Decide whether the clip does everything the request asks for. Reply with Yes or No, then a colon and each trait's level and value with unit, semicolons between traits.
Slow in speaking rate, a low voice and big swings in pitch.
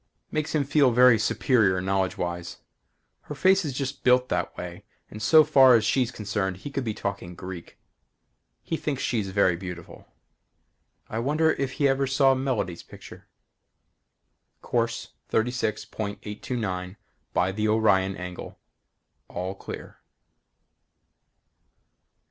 Yes: slow, 120 wpm; low, 110 Hz; wide, 5.9 semitones